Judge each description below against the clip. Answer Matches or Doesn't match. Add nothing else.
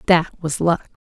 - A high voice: Doesn't match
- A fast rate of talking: Doesn't match